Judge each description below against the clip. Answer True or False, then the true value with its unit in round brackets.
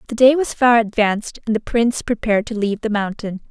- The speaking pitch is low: False (225 Hz)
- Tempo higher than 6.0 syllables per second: True (6.3 syllables/s)